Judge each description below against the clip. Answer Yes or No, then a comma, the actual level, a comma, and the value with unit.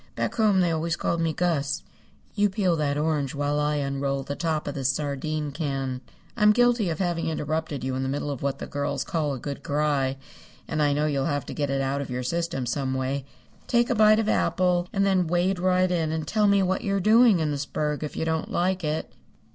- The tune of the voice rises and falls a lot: No, average, 4.3 semitones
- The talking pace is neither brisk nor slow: No, fast, 230 wpm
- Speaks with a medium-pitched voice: Yes, medium, 155 Hz